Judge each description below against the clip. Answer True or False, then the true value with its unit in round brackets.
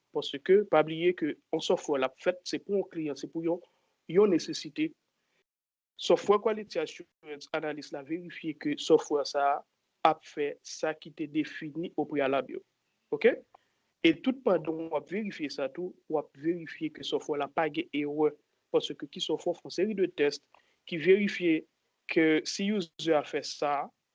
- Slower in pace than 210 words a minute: True (165 wpm)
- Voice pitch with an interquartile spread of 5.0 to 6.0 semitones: True (5.3 semitones)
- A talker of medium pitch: True (165 Hz)